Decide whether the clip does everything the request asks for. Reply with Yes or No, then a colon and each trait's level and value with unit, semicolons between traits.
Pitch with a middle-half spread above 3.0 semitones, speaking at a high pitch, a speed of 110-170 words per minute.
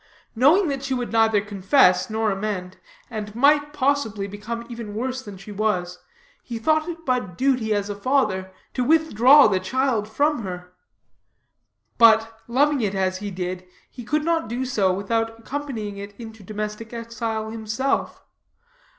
Yes: average, 4.2 semitones; high, 225 Hz; average, 155 wpm